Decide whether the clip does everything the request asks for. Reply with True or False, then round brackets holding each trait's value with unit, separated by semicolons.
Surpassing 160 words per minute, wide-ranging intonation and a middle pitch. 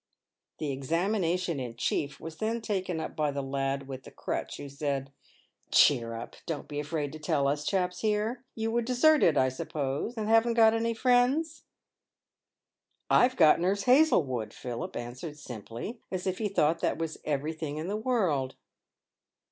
True (170 wpm; 8.0 semitones; 165 Hz)